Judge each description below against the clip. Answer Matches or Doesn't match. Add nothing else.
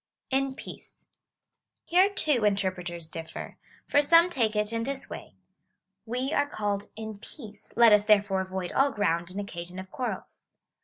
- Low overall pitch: Doesn't match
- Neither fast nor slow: Matches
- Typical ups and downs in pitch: Doesn't match